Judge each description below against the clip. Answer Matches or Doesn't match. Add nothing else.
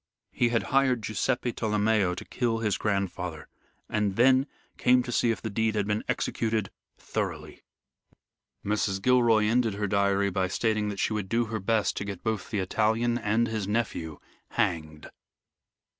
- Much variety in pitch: Doesn't match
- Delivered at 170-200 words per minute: Doesn't match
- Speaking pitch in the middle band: Doesn't match